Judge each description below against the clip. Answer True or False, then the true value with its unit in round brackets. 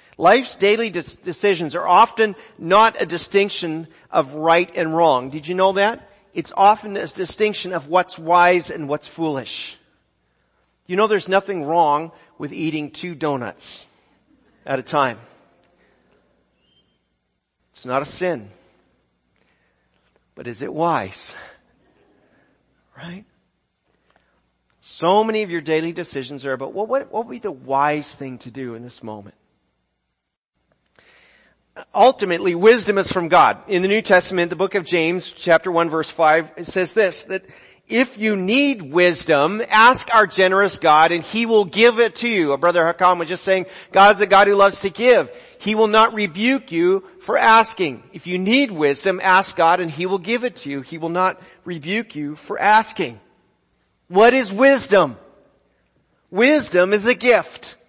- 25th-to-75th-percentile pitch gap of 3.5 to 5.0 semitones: True (4.6 semitones)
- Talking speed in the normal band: True (160 wpm)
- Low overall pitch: False (180 Hz)